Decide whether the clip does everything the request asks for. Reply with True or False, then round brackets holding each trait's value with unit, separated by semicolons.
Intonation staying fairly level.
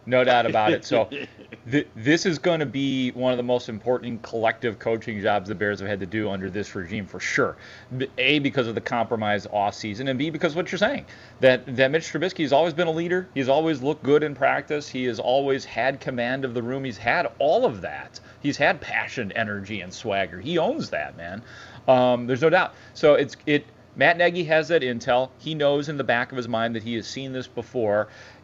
False (4.2 semitones)